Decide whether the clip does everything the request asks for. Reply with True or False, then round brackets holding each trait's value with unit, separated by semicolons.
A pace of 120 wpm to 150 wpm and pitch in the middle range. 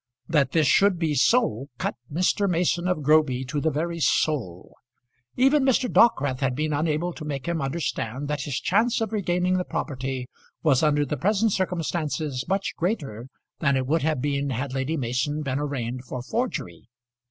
False (175 wpm; 150 Hz)